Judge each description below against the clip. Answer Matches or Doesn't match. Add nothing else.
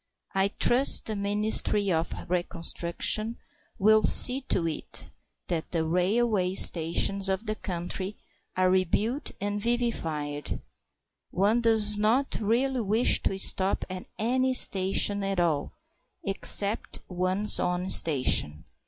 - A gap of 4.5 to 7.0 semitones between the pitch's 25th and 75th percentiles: Doesn't match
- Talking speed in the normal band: Doesn't match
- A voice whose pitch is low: Doesn't match